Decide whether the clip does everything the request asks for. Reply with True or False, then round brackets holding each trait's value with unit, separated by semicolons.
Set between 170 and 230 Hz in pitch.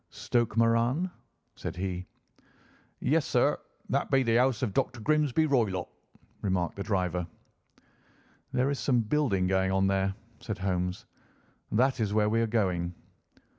False (110 Hz)